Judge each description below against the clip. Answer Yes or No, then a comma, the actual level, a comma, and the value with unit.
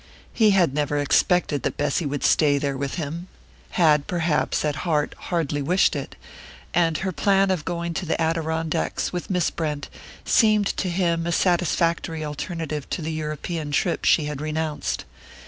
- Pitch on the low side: No, medium, 160 Hz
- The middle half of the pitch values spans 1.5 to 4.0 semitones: Yes, average, 2.8 semitones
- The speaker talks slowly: No, average, 165 wpm